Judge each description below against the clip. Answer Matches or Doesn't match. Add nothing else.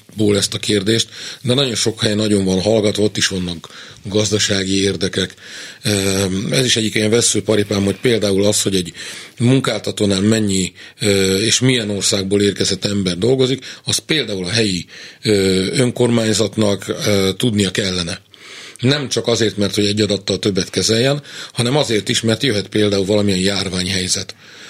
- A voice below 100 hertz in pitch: Doesn't match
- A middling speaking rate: Matches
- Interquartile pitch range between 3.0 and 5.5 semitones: Doesn't match